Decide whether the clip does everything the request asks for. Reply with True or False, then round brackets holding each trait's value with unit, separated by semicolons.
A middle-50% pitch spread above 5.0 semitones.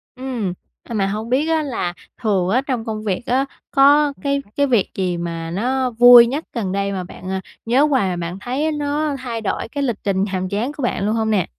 True (5.4 semitones)